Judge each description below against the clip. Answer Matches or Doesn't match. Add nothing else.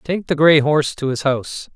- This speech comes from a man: Matches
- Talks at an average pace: Doesn't match